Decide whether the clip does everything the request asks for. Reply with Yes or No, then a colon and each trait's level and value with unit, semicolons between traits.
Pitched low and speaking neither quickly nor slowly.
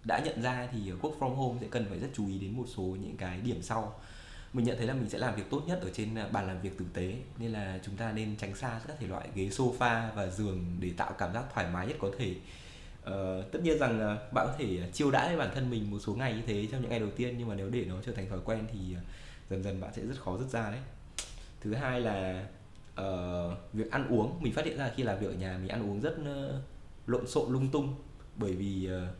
No: low, 110 Hz; fast, 270 wpm